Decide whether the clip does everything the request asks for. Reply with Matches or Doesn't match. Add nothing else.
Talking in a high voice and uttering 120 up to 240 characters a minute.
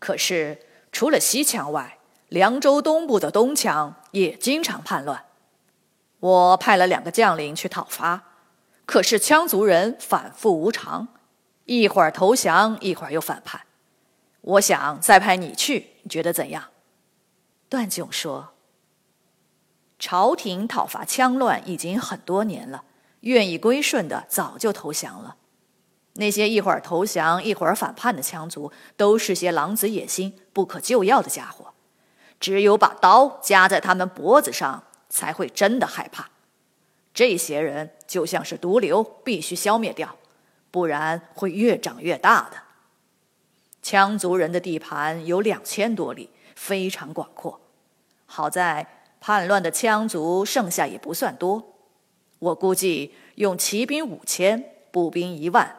Matches